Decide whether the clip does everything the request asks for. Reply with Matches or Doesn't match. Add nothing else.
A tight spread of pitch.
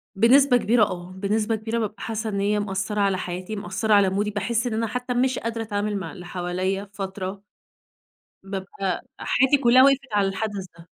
Doesn't match